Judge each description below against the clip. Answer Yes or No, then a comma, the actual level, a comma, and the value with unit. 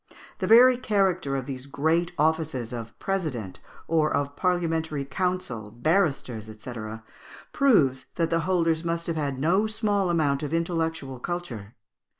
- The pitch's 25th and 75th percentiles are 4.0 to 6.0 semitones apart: Yes, average, 4.7 semitones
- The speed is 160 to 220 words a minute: No, average, 140 wpm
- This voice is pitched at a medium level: Yes, medium, 160 Hz